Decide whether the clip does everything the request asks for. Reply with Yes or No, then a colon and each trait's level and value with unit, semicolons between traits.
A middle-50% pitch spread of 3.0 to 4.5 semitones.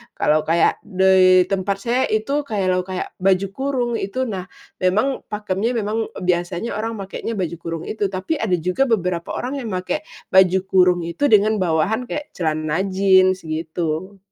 Yes: average, 3.4 semitones